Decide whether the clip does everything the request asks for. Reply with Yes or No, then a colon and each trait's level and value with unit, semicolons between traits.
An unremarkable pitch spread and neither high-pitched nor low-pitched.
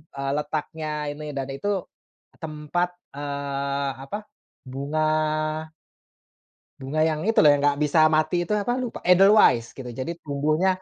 Yes: average, 3.0 semitones; medium, 155 Hz